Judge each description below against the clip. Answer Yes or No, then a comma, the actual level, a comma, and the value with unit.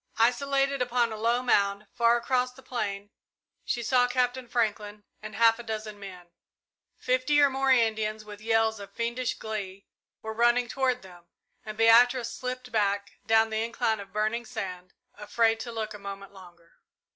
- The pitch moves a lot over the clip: No, average, 2.9 semitones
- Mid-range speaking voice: No, high, 225 Hz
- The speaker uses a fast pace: No, average, 165 wpm